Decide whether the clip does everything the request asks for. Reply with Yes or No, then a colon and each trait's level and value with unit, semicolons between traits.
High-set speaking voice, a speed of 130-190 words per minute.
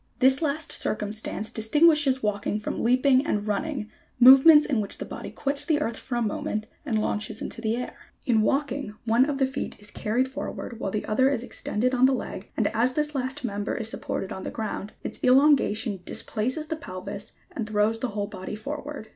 No: high, 240 Hz; fast, 205 wpm